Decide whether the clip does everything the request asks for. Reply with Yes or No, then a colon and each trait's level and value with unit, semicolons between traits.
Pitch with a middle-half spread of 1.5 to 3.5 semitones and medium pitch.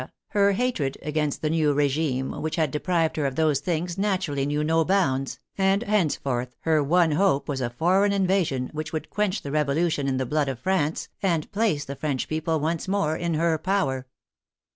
No: average, 4.3 semitones; medium, 155 Hz